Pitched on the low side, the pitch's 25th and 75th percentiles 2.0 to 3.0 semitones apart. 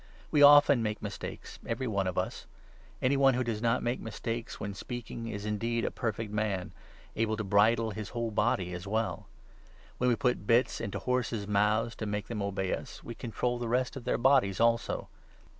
Yes: low, 115 Hz; average, 2.7 semitones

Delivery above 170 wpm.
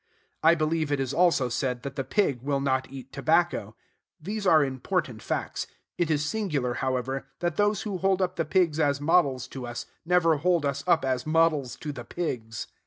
Yes: average, 190 wpm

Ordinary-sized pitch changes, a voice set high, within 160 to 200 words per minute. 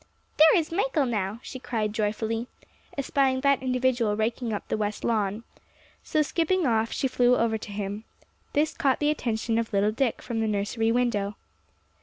Yes: average, 3.6 semitones; high, 230 Hz; average, 170 wpm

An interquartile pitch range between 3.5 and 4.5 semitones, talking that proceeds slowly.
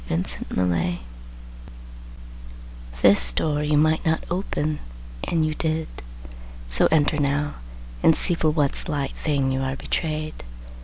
No: average, 2.8 semitones; slow, 125 wpm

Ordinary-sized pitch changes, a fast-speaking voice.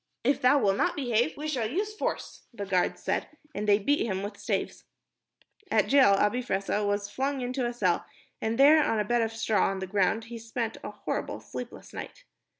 Yes: average, 4.3 semitones; fast, 210 wpm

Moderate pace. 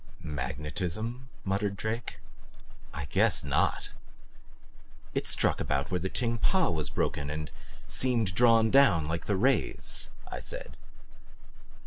No: slow, 120 wpm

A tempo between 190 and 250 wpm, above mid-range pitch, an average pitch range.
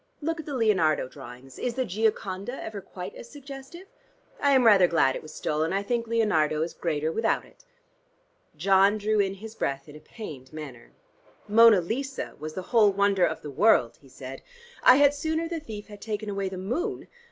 No: average, 195 wpm; high, 200 Hz; wide, 6.9 semitones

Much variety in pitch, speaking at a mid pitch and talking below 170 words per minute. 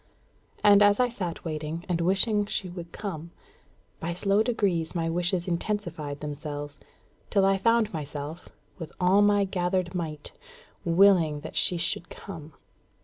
No: average, 3.7 semitones; medium, 175 Hz; average, 145 wpm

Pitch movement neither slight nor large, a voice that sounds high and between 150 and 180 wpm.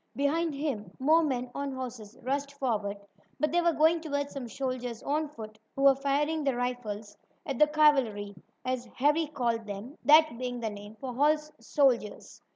Yes: average, 4.2 semitones; very high, 270 Hz; average, 170 wpm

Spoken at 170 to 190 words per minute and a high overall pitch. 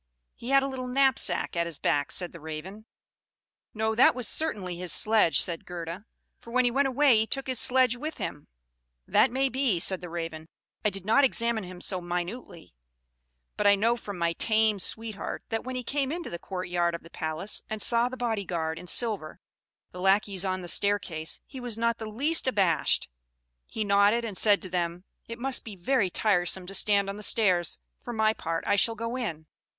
No: fast, 205 wpm; high, 205 Hz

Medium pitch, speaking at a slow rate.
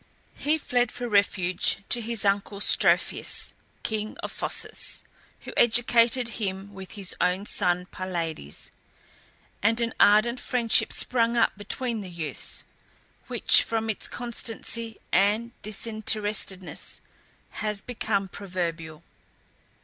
No: high, 210 Hz; slow, 110 wpm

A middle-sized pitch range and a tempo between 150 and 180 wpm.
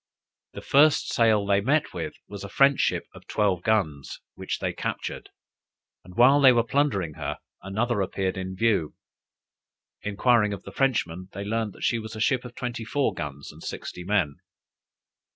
Yes: average, 4.5 semitones; average, 170 wpm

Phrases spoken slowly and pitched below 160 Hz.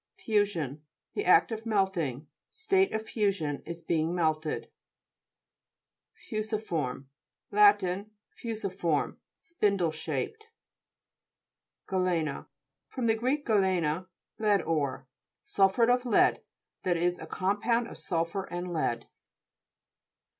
No: slow, 105 wpm; high, 190 Hz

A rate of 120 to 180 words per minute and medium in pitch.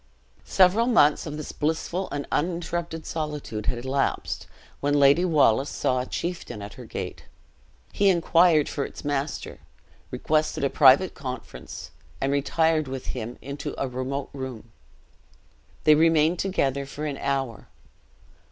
Yes: slow, 135 wpm; medium, 145 Hz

